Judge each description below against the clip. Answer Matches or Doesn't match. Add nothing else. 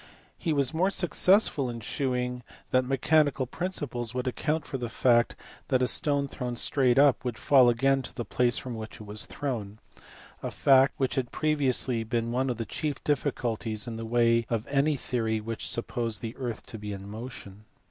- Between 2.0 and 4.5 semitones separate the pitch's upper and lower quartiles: Matches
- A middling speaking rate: Matches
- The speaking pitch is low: Matches